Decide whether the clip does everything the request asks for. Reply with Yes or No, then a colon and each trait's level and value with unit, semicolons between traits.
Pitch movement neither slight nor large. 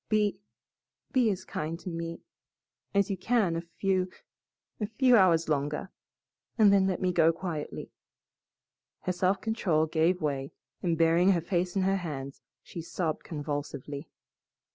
Yes: average, 3.4 semitones